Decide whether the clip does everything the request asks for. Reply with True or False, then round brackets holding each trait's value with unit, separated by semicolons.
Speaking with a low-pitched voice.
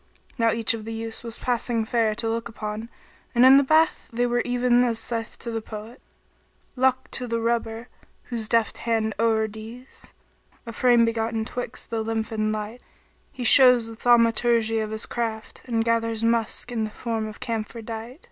False (230 Hz)